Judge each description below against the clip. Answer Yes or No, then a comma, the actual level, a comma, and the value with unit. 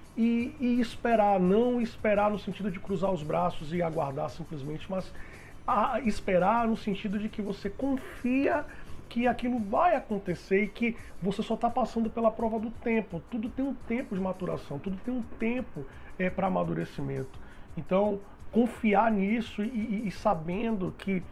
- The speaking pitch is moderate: No, high, 210 Hz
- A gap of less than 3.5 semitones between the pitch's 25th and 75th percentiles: No, average, 4.0 semitones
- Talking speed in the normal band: Yes, average, 165 wpm